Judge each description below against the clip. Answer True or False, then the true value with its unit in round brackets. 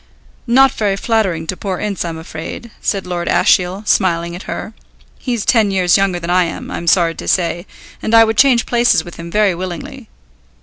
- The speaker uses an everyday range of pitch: True (4.0 semitones)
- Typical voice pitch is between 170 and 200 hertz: True (185 Hz)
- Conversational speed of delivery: True (190 wpm)